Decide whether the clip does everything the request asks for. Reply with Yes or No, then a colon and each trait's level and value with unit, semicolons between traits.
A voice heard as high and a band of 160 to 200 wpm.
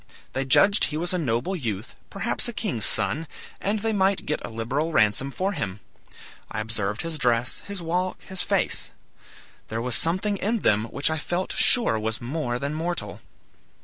No: medium, 155 Hz; average, 180 wpm